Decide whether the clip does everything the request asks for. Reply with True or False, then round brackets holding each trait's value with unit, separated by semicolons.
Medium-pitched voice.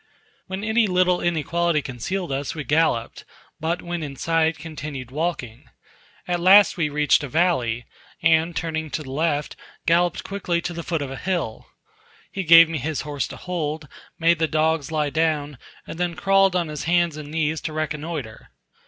True (160 Hz)